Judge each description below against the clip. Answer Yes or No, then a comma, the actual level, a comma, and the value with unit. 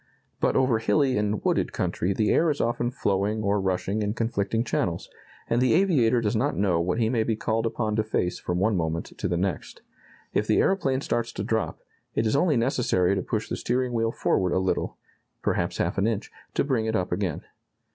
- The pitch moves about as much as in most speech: Yes, average, 3.5 semitones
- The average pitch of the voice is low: Yes, low, 110 Hz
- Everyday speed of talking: No, fast, 210 wpm